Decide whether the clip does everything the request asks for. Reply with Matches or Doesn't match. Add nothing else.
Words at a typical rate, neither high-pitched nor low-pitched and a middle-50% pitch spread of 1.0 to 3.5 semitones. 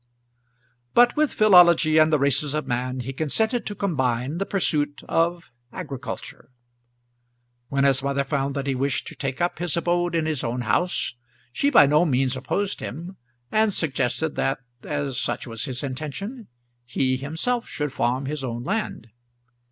Doesn't match